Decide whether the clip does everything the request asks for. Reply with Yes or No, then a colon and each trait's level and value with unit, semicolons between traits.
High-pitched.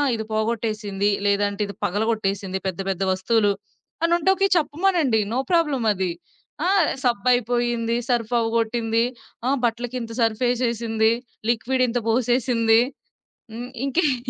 Yes: high, 230 Hz